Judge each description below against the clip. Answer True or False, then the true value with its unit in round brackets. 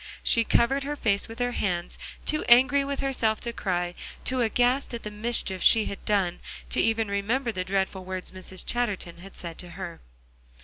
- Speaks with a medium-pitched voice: False (215 Hz)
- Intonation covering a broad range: False (4.5 semitones)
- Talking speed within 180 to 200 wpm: True (185 wpm)